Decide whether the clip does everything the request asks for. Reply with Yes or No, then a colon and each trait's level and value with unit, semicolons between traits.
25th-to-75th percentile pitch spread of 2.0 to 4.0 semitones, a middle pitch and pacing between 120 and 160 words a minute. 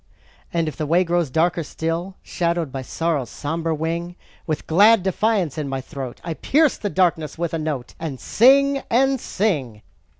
No: average, 3.7 semitones; medium, 165 Hz; average, 170 wpm